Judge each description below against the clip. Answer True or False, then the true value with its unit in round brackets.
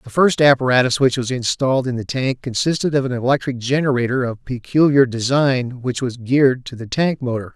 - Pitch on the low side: True (130 Hz)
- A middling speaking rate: True (190 wpm)